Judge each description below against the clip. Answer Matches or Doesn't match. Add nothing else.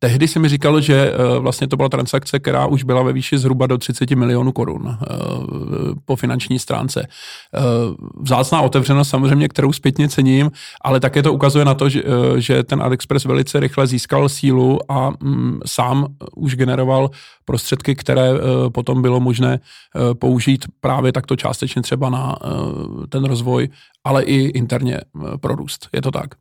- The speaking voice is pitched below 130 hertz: Doesn't match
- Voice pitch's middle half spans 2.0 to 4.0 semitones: Doesn't match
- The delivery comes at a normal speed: Matches